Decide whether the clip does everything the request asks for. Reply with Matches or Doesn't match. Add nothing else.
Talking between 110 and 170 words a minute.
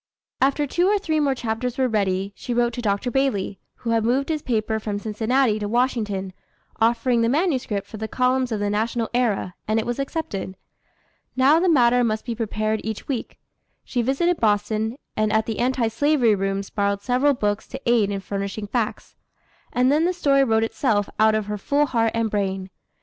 Doesn't match